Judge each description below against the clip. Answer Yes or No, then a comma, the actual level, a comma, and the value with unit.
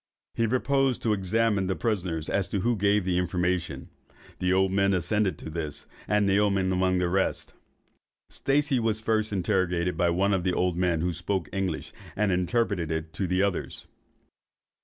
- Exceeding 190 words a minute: No, average, 165 wpm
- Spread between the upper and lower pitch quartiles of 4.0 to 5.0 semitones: No, average, 2.8 semitones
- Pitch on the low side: Yes, very low, 95 Hz